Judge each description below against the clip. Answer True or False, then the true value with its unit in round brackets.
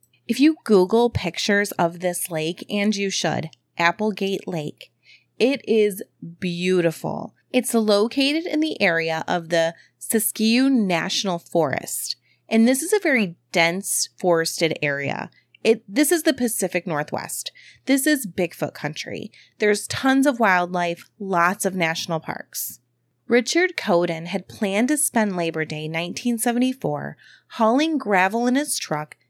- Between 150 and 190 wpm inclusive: False (135 wpm)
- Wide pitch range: True (6.2 semitones)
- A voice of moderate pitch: False (200 Hz)